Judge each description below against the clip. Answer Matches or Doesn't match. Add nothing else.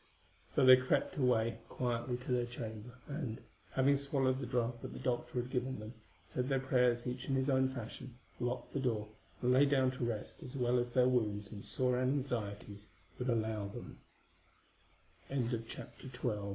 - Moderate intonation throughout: Doesn't match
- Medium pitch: Doesn't match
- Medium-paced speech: Matches